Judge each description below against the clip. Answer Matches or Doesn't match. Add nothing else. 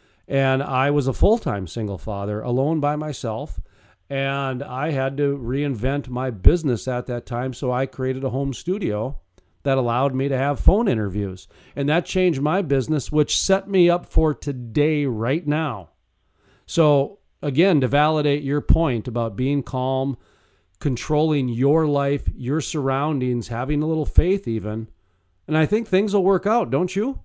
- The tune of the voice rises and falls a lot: Doesn't match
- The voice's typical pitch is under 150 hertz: Matches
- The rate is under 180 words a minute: Matches